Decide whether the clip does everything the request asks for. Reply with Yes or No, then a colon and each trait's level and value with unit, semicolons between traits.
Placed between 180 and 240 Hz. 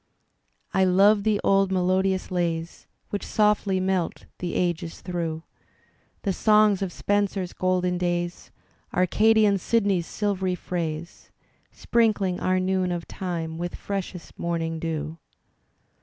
Yes: medium, 185 Hz